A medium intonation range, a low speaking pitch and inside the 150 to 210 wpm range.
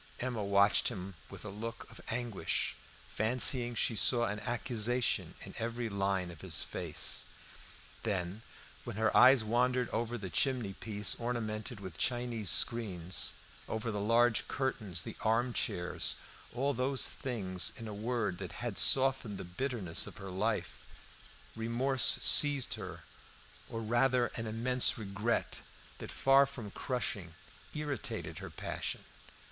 No: average, 3.5 semitones; low, 115 Hz; slow, 135 wpm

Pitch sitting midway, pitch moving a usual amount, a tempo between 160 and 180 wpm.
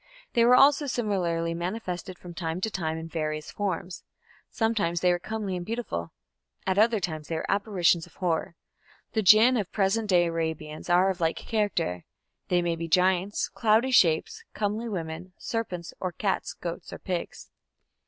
Yes: medium, 180 Hz; average, 4.3 semitones; average, 165 wpm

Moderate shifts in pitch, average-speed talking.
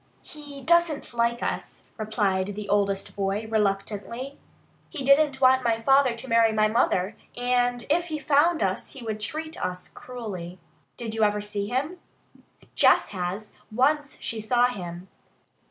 Yes: average, 4.8 semitones; average, 150 wpm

